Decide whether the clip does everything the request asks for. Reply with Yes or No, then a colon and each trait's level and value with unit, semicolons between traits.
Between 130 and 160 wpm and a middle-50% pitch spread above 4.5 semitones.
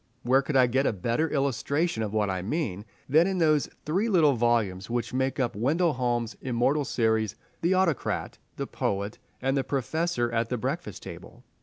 No: average, 175 wpm; average, 5.0 semitones